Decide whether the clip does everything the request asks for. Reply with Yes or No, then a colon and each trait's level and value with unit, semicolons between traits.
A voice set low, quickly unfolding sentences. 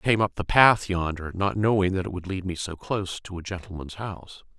Yes: very low, 95 Hz; fast, 250 wpm